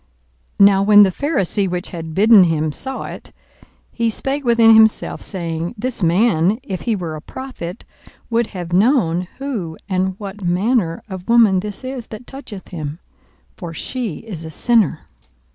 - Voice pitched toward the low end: No, high, 200 Hz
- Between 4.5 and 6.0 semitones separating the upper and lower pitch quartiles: Yes, average, 5.0 semitones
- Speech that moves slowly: No, average, 160 wpm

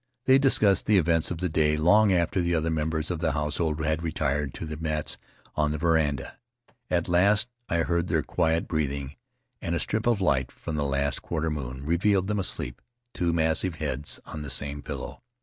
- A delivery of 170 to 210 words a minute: Yes, average, 195 wpm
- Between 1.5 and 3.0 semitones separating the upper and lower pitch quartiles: Yes, average, 2.7 semitones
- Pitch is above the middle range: No, very low, 80 Hz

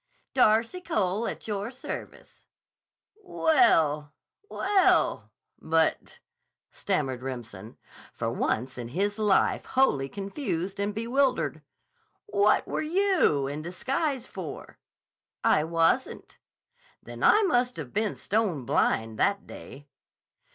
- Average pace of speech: No, slow, 100 wpm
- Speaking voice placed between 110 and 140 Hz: No, high, 200 Hz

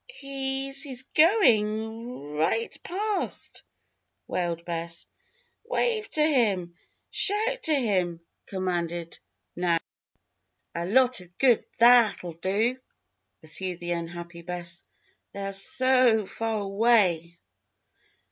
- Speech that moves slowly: Yes, slow, 120 wpm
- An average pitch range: No, wide, 7.1 semitones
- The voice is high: Yes, high, 210 Hz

